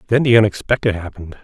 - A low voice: Yes, low, 105 Hz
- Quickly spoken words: No, average, 165 wpm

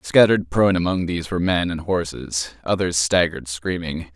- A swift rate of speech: No, average, 160 wpm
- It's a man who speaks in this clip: Yes, male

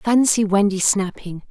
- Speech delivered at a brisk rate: No, slow, 120 wpm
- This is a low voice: No, high, 200 Hz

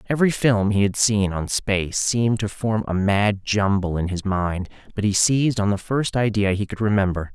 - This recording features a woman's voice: No, male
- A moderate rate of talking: No, fast, 210 wpm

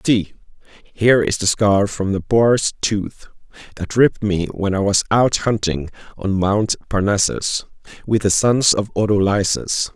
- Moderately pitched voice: No, low, 105 Hz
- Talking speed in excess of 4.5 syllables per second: No, 4.2 syllables/s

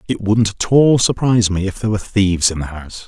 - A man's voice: Yes, male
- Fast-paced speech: Yes, fast, 255 wpm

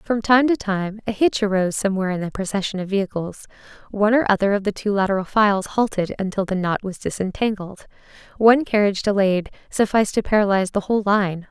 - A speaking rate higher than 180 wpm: Yes, average, 190 wpm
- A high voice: Yes, high, 200 Hz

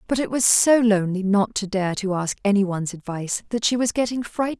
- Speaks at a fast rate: Yes, fast, 220 wpm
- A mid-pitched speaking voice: No, high, 210 Hz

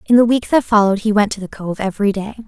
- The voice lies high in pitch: Yes, high, 210 Hz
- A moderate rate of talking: No, fast, 290 wpm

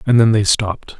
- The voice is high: No, low, 110 Hz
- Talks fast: Yes, fast, 240 wpm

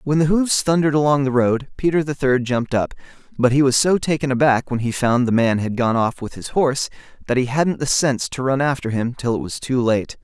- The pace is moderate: No, fast, 250 wpm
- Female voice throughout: No, male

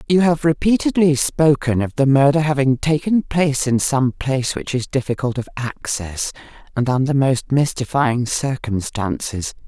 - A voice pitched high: No, low, 135 Hz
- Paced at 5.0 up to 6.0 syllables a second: No, 4.6 syllables/s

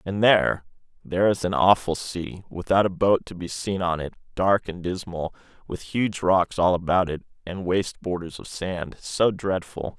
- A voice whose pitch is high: No, very low, 90 Hz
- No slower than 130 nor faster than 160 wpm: No, average, 185 wpm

